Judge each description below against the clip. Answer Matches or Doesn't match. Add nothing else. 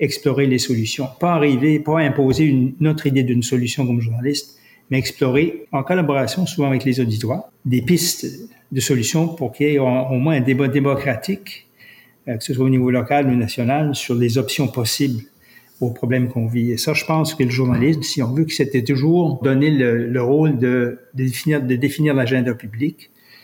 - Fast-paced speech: Doesn't match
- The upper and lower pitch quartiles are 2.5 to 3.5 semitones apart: Matches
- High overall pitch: Doesn't match